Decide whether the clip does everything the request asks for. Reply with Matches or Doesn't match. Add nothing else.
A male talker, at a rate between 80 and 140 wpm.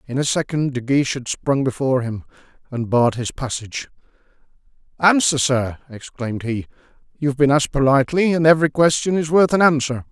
Doesn't match